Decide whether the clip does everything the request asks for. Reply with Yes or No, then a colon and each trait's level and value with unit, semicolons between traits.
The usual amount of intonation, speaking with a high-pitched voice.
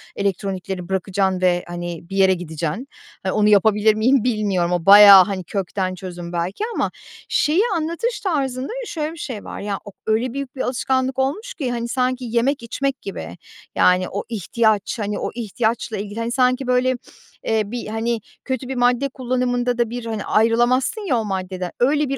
Yes: average, 4.8 semitones; high, 225 Hz